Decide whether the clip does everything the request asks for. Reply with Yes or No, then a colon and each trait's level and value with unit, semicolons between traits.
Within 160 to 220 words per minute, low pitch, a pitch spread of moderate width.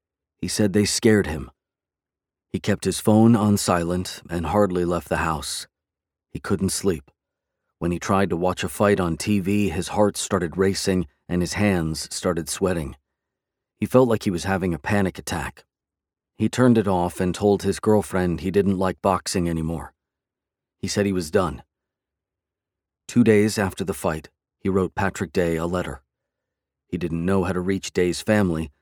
Yes: average, 175 wpm; very low, 95 Hz; average, 3.1 semitones